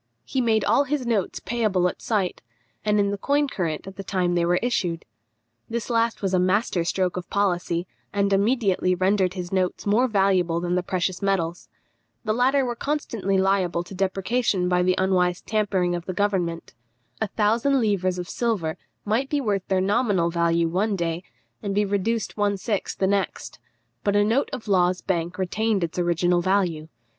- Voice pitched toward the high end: Yes, high, 195 Hz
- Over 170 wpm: Yes, average, 180 wpm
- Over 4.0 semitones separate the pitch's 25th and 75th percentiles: No, average, 3.2 semitones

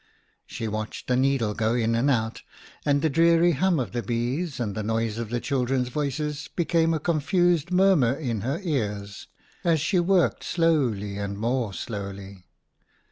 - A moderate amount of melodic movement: No, wide, 6.3 semitones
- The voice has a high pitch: No, low, 130 Hz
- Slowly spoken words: No, average, 165 wpm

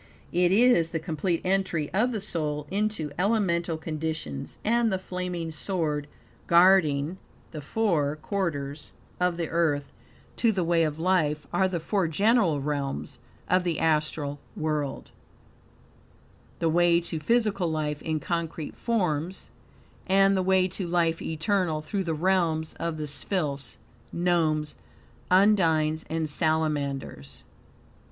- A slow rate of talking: Yes, slow, 130 wpm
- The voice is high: No, medium, 165 Hz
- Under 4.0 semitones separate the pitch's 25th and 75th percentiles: Yes, average, 3.5 semitones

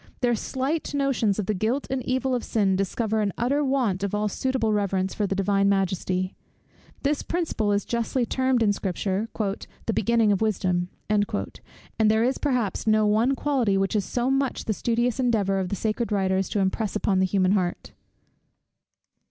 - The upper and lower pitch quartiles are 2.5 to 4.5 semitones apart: Yes, average, 4.0 semitones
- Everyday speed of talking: Yes, average, 180 wpm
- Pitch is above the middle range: Yes, high, 215 Hz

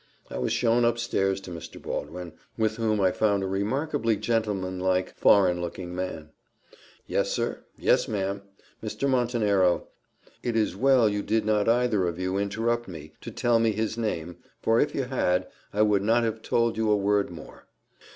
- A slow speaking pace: No, average, 175 wpm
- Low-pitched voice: Yes, low, 105 Hz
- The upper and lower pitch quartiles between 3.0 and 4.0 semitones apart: Yes, average, 3.6 semitones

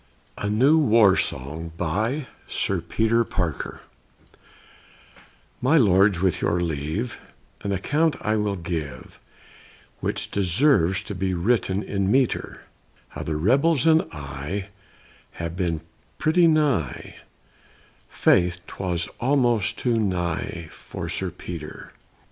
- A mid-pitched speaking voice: No, very low, 95 Hz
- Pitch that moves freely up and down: Yes, wide, 6.1 semitones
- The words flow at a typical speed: No, slow, 115 wpm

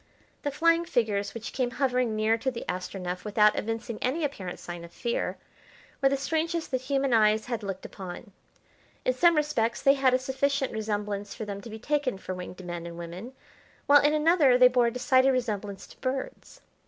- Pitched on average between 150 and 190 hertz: No, high, 240 Hz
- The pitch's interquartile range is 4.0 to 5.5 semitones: Yes, average, 4.8 semitones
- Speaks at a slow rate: No, average, 190 wpm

